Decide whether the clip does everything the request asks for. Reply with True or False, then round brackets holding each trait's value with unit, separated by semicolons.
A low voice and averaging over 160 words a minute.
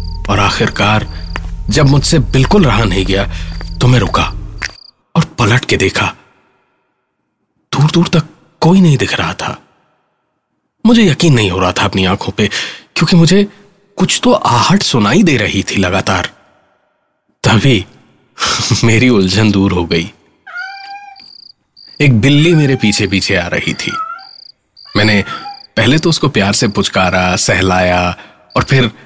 False (120 Hz; 135 wpm)